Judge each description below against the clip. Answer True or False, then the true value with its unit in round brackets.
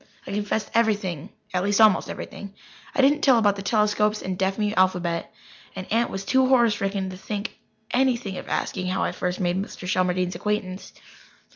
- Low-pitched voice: False (200 Hz)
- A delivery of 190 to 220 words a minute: False (175 wpm)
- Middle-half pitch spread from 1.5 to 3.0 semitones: True (2.7 semitones)